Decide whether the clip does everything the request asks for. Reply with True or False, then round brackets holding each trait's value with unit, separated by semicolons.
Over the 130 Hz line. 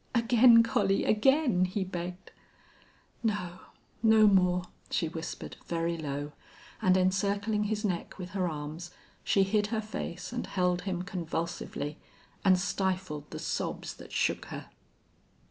True (185 Hz)